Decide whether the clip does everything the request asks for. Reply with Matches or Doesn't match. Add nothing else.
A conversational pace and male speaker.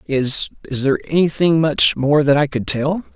Matches